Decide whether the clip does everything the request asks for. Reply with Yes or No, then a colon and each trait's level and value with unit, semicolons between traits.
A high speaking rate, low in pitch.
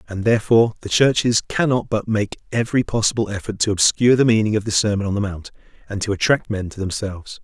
Yes: fast, 210 wpm; low, 110 Hz